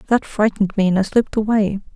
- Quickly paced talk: Yes, fast, 215 wpm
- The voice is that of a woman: Yes, female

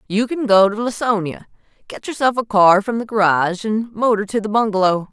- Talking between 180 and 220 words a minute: Yes, average, 200 wpm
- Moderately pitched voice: No, high, 210 Hz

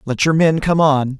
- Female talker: No, male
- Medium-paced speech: No, fast, 250 wpm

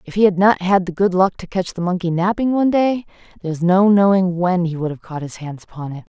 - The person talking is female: Yes, female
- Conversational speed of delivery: No, fast, 275 wpm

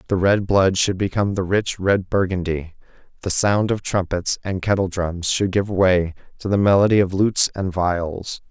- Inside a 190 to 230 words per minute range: No, average, 175 wpm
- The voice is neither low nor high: No, very low, 95 Hz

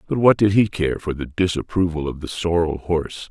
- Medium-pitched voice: No, very low, 85 Hz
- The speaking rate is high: Yes, fast, 220 wpm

